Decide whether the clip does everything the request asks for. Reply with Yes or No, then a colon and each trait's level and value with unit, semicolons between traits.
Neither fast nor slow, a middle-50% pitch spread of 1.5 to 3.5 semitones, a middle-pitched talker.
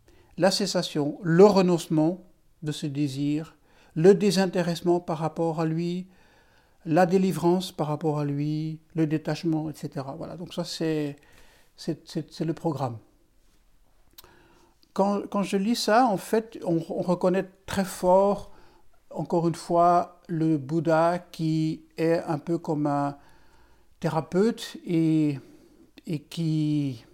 No: slow, 130 wpm; average, 2.8 semitones; medium, 165 Hz